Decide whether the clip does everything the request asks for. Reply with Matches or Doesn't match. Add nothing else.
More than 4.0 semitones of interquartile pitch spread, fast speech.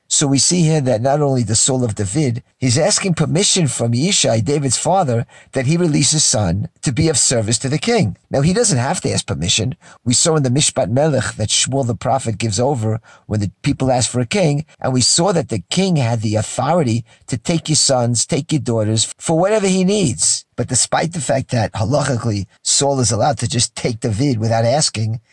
Matches